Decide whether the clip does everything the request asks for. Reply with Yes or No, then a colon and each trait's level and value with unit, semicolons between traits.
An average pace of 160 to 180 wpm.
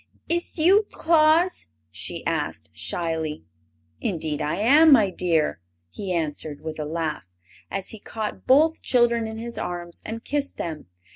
No: average, 145 wpm